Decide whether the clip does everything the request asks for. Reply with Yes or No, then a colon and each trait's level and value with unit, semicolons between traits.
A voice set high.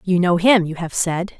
No: medium, 180 Hz